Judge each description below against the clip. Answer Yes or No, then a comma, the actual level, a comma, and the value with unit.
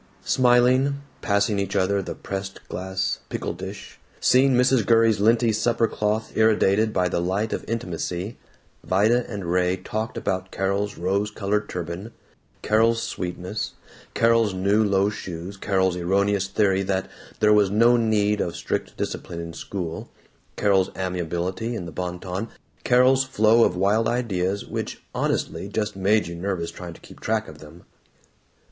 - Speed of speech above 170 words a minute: No, average, 155 wpm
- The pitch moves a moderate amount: Yes, average, 3.2 semitones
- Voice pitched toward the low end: Yes, low, 100 Hz